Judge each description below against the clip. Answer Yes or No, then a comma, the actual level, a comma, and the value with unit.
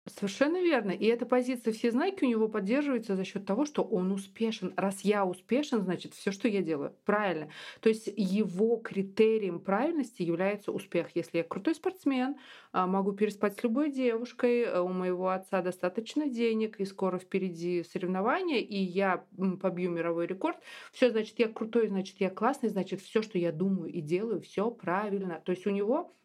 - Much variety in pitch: No, average, 4.3 semitones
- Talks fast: Yes, fast, 170 wpm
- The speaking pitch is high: Yes, high, 200 Hz